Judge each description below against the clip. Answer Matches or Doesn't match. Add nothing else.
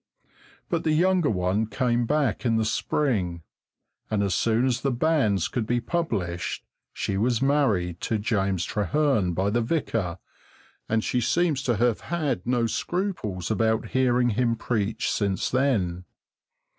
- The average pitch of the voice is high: Doesn't match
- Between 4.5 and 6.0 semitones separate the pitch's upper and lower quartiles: Matches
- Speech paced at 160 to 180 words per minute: Doesn't match